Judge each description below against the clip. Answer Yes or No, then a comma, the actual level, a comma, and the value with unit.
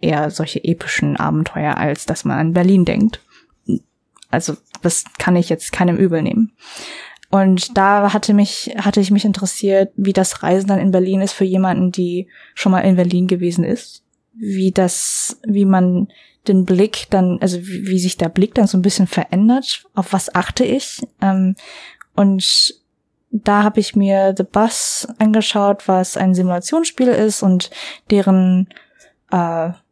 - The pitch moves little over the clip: Yes, narrow, 2.3 semitones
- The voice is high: Yes, high, 195 Hz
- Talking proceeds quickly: No, average, 160 wpm